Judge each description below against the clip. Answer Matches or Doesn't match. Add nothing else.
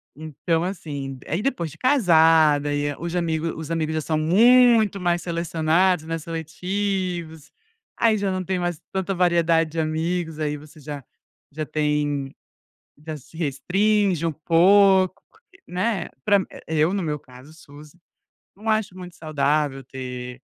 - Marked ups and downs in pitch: Doesn't match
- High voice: Doesn't match